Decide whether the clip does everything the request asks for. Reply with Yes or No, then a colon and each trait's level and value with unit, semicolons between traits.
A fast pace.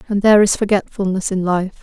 No: average, 195 wpm